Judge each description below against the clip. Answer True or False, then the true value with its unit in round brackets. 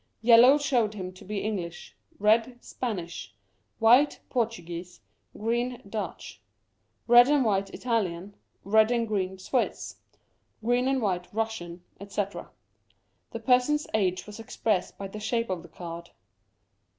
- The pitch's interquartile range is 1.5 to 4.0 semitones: False (4.4 semitones)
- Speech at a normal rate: False (125 wpm)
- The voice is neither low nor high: False (215 Hz)